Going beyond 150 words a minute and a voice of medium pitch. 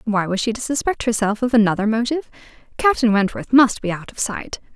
No: average, 200 wpm; high, 230 Hz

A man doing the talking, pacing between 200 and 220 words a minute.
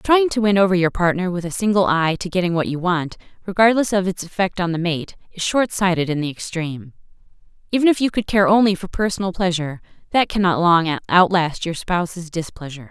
No: female; fast, 205 wpm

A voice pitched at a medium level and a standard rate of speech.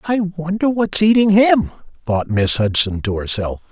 Yes: medium, 160 Hz; average, 160 wpm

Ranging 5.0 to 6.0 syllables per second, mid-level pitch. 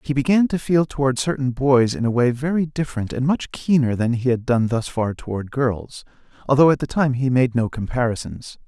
No: 5.4 syllables/s; low, 130 Hz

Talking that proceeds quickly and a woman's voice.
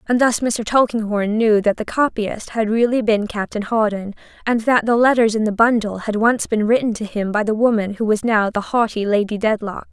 Yes: fast, 220 wpm; female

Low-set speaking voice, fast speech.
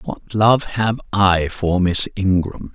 No: very low, 95 Hz; average, 155 wpm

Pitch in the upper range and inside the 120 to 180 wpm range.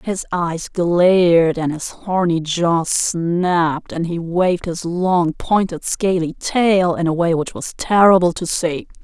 No: medium, 175 Hz; average, 160 wpm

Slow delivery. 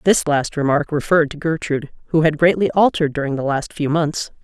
No: fast, 205 wpm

